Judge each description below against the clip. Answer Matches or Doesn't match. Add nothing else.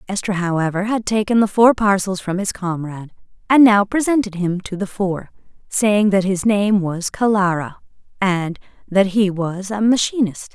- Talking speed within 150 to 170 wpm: Matches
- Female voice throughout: Matches